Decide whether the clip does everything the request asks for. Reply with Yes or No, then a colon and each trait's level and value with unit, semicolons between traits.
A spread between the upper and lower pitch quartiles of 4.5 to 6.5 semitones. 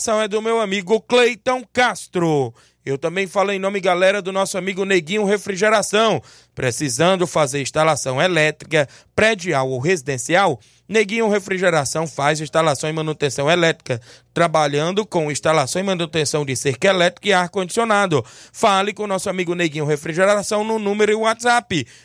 Yes: average, 5.1 semitones